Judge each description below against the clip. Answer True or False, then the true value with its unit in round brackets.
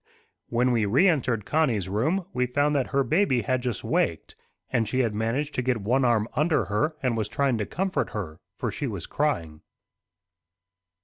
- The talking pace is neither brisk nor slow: True (180 wpm)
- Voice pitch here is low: True (125 Hz)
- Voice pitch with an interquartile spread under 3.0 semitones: False (4.7 semitones)